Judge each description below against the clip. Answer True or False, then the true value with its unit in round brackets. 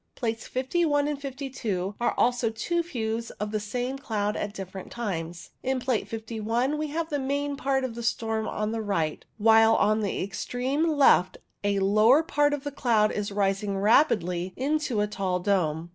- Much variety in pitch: False (4.9 semitones)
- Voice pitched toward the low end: False (225 Hz)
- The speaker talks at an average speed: True (175 wpm)